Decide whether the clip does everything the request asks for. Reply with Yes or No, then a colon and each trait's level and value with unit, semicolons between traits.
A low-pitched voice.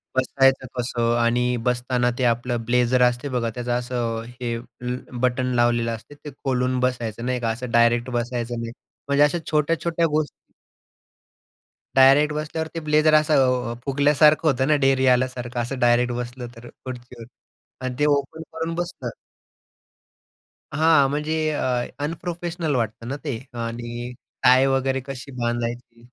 Yes: low, 125 Hz